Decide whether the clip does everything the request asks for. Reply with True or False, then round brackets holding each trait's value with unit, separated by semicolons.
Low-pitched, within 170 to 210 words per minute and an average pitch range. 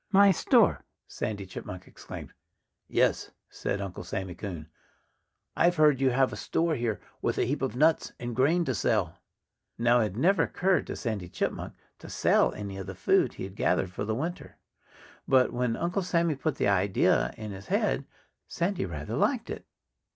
False (120 Hz; 180 wpm; 8.2 semitones)